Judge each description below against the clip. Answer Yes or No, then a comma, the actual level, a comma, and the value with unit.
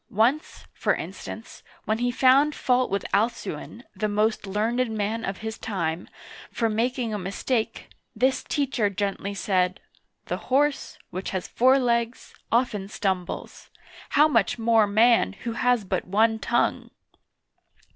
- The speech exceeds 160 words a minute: No, average, 150 wpm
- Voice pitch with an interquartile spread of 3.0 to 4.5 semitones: Yes, average, 3.5 semitones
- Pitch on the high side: Yes, high, 225 Hz